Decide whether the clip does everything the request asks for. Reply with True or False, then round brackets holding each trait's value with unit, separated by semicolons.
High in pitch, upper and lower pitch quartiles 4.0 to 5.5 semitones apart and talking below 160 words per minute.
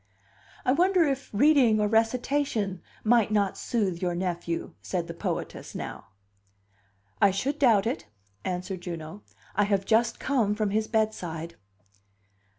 True (210 Hz; 4.5 semitones; 135 wpm)